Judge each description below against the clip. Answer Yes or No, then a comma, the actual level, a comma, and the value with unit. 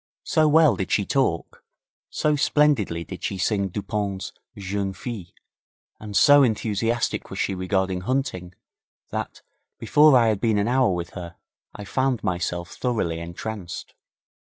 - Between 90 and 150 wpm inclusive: Yes, average, 140 wpm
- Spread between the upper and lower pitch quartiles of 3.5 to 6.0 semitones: Yes, average, 5.2 semitones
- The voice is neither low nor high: No, low, 100 Hz